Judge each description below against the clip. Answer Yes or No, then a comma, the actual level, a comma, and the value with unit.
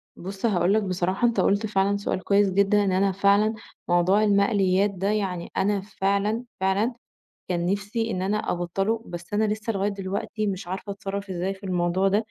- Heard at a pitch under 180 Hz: No, high, 200 Hz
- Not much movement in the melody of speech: Yes, narrow, 1.8 semitones